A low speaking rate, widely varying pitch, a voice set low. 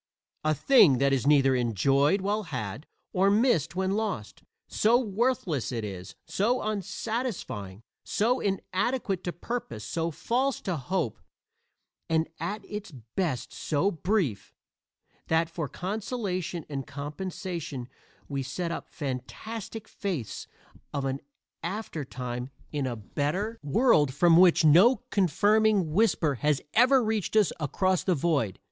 No: slow, 125 wpm; wide, 7.2 semitones; medium, 170 Hz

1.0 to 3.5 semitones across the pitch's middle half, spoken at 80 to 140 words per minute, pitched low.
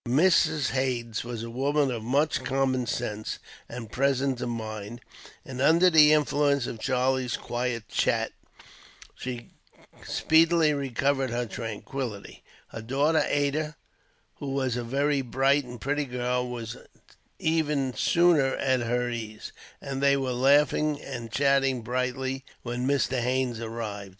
Yes: average, 2.8 semitones; slow, 135 wpm; low, 130 Hz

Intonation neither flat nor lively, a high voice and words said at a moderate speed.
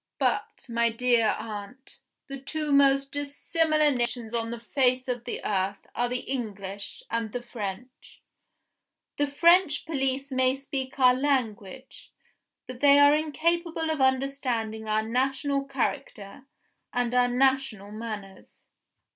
No: average, 3.4 semitones; very high, 255 Hz; slow, 130 wpm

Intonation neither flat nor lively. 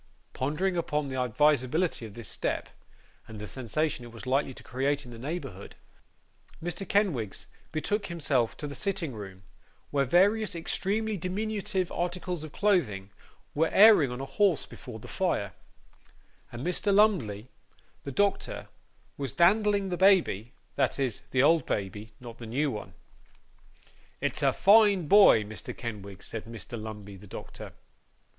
No: wide, 8.2 semitones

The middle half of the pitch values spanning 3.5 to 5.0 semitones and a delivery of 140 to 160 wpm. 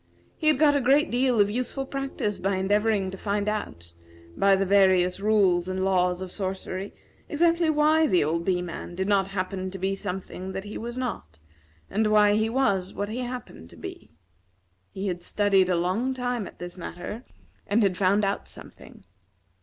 No: average, 4.1 semitones; average, 185 wpm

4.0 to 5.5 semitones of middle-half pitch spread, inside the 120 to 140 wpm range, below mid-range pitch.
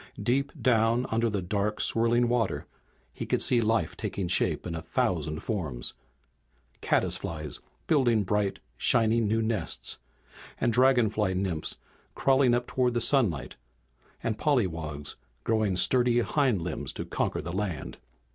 Yes: average, 4.8 semitones; slow, 135 wpm; low, 110 Hz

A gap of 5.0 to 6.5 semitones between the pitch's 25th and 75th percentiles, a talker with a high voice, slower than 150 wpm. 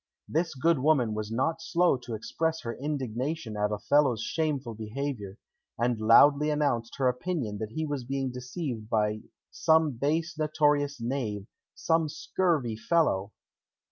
No: wide, 5.5 semitones; low, 135 Hz; average, 140 wpm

